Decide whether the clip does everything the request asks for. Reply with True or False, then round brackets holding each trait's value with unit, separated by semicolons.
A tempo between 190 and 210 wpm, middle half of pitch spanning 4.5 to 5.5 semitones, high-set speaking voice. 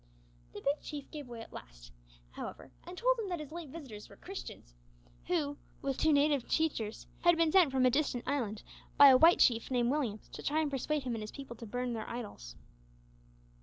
True (205 wpm; 4.8 semitones; 275 Hz)